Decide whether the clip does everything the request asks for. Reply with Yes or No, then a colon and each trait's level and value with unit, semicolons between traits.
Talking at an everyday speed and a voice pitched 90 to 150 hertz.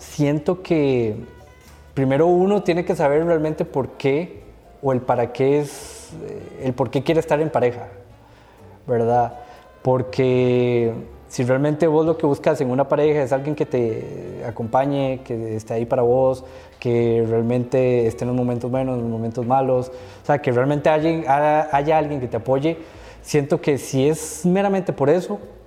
Yes: average, 170 wpm; low, 135 Hz